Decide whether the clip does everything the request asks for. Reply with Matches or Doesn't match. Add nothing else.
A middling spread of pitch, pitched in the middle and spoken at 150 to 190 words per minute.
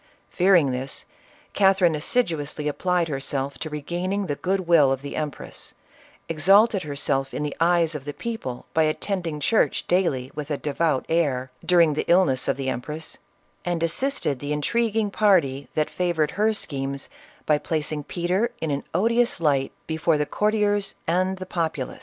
Matches